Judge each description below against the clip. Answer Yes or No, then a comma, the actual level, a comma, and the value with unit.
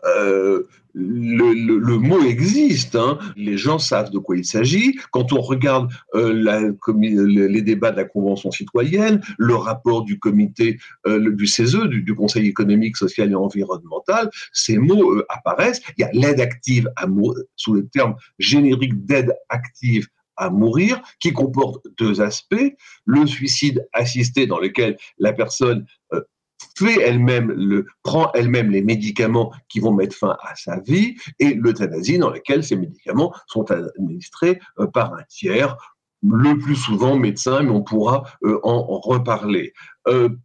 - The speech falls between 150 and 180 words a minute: Yes, average, 155 wpm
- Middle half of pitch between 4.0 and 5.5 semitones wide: Yes, average, 4.4 semitones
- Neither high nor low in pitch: No, low, 120 Hz